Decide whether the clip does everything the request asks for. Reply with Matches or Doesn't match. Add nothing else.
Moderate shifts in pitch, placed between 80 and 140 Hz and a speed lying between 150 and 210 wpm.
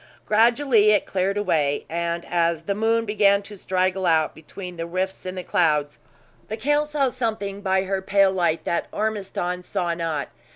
Doesn't match